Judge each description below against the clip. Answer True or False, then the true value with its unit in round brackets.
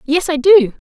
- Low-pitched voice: False (310 Hz)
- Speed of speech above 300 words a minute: False (205 wpm)